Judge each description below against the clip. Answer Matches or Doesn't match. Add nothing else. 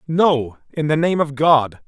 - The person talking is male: Matches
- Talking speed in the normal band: Matches